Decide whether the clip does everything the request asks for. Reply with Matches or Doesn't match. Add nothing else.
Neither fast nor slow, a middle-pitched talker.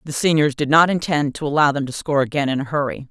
Doesn't match